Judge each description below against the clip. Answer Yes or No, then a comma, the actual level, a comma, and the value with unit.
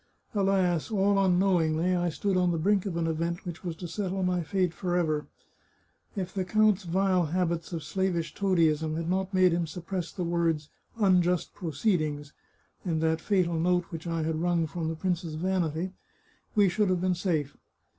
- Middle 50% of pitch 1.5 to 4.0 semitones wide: Yes, narrow, 2.5 semitones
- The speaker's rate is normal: Yes, average, 180 wpm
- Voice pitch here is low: No, medium, 175 Hz